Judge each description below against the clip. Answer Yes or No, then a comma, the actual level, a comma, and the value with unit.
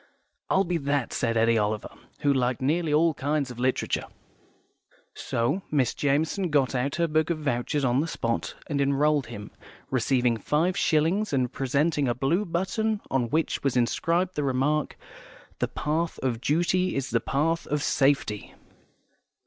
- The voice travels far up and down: No, average, 4.4 semitones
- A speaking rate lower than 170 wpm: Yes, average, 155 wpm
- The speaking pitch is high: No, medium, 145 Hz